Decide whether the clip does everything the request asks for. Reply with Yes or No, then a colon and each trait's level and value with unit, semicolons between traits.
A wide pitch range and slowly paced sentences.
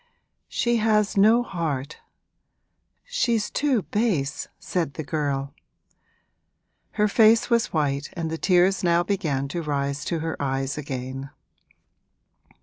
Yes: wide, 7.1 semitones; slow, 120 wpm